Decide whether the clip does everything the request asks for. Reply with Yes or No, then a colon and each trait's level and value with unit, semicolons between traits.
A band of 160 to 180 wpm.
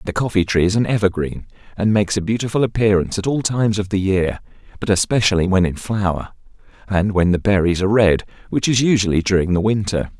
No: average, 200 wpm